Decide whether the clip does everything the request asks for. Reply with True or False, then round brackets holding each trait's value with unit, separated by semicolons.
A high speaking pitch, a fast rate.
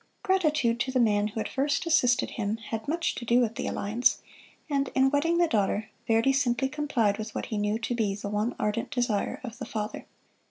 True (235 Hz; 210 wpm)